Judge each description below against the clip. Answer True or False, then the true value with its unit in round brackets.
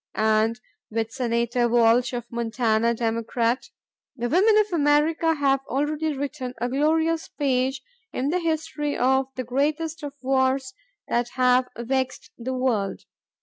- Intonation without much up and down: False (3.8 semitones)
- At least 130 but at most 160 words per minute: True (135 wpm)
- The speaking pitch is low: False (260 Hz)